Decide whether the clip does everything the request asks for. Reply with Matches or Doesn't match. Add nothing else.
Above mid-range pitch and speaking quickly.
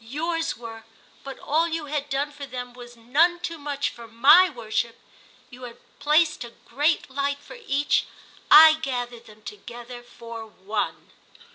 Doesn't match